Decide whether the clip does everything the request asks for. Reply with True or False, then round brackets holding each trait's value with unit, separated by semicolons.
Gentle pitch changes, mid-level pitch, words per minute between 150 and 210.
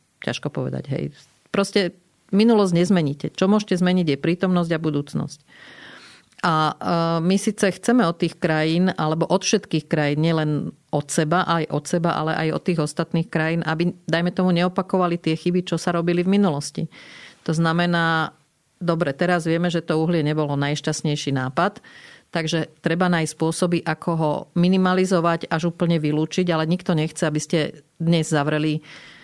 True (2.3 semitones; 170 Hz; 155 wpm)